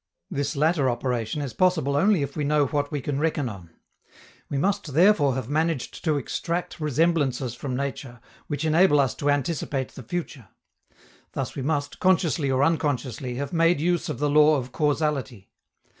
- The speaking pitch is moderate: Yes, medium, 145 Hz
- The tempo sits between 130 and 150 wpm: No, average, 170 wpm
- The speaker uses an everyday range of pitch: Yes, average, 3.2 semitones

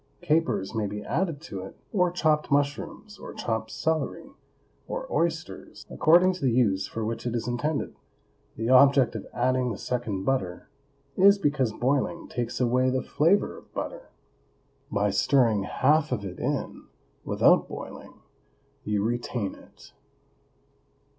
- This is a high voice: No, low, 130 Hz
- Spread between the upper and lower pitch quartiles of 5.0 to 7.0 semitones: Yes, wide, 5.4 semitones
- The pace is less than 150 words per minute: Yes, average, 140 wpm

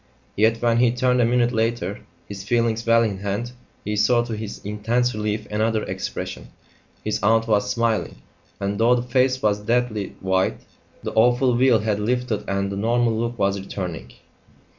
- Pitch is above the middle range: No, low, 110 Hz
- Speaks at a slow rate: No, average, 170 wpm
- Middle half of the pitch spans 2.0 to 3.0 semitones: Yes, average, 2.7 semitones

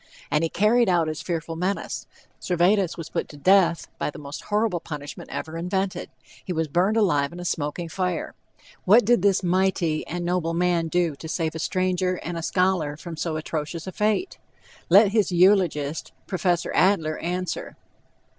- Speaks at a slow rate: No, average, 175 wpm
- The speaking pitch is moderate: Yes, medium, 175 Hz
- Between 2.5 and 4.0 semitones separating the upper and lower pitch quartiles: Yes, average, 2.8 semitones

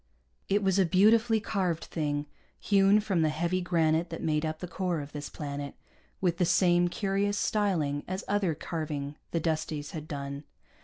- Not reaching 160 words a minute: No, average, 170 wpm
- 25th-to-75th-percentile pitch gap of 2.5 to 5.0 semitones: Yes, average, 4.2 semitones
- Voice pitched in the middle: Yes, medium, 170 Hz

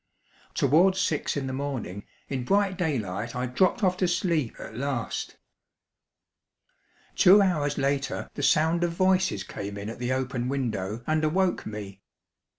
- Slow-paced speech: No, average, 150 wpm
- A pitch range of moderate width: No, wide, 6.6 semitones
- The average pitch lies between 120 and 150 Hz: Yes, medium, 140 Hz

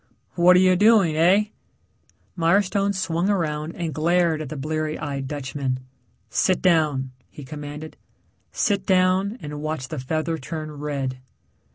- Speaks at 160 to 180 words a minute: No, average, 140 wpm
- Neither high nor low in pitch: Yes, medium, 160 Hz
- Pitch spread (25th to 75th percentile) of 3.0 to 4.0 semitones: Yes, average, 3.7 semitones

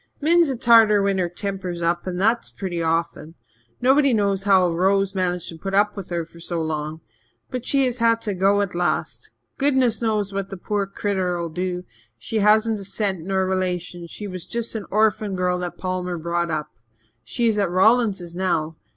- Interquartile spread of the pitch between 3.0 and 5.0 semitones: Yes, average, 3.4 semitones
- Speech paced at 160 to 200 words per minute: Yes, average, 190 wpm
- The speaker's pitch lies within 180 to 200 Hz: Yes, high, 190 Hz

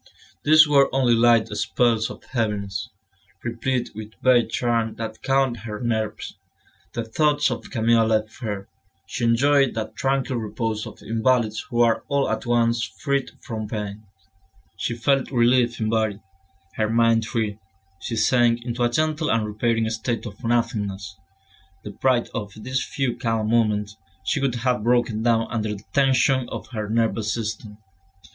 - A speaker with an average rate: Yes, average, 150 wpm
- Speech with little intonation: Yes, narrow, 2.3 semitones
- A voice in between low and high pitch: No, low, 115 Hz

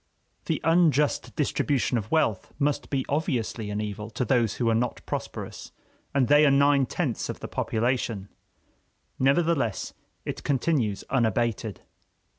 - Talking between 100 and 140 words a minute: Yes, slow, 135 wpm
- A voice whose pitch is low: Yes, low, 130 Hz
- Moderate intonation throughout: Yes, average, 4.3 semitones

